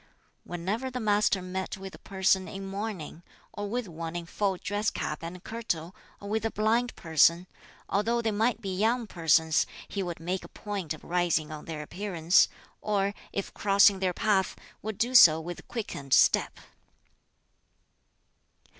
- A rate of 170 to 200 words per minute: No, average, 160 wpm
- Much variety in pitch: No, average, 3.8 semitones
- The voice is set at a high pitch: Yes, high, 195 Hz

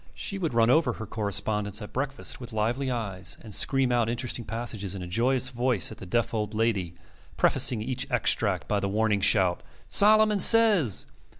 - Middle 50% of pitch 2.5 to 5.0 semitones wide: Yes, average, 3.9 semitones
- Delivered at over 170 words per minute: Yes, average, 180 wpm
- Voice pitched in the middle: No, low, 115 Hz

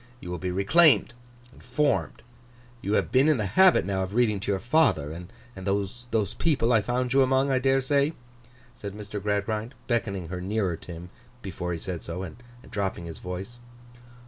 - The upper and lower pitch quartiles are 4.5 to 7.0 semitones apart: Yes, average, 5.2 semitones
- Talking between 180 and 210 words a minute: Yes, average, 185 wpm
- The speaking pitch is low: Yes, low, 105 Hz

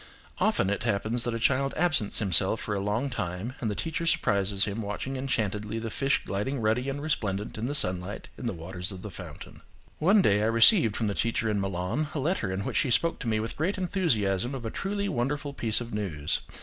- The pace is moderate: No, fast, 220 wpm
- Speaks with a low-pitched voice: Yes, low, 110 Hz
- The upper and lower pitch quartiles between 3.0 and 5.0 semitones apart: No, wide, 5.4 semitones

